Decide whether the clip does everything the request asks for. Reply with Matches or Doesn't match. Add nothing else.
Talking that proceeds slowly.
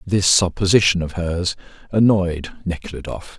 Matches